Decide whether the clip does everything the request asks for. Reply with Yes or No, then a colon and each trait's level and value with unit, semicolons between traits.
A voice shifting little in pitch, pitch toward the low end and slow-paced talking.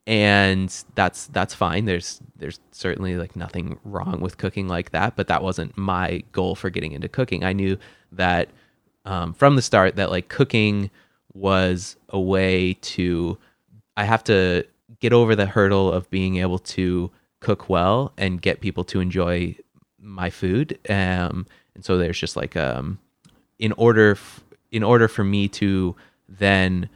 No: narrow, 2.2 semitones; very low, 95 Hz; average, 160 wpm